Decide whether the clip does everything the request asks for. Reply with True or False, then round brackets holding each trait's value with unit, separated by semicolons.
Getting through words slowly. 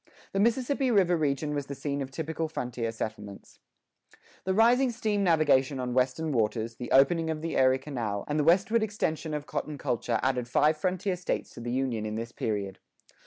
False (185 wpm)